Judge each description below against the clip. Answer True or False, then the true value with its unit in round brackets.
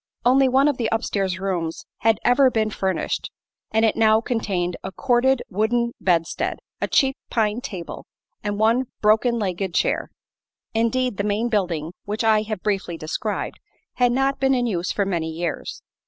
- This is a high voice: True (215 Hz)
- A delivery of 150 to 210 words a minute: True (165 wpm)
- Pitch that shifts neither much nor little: True (4.1 semitones)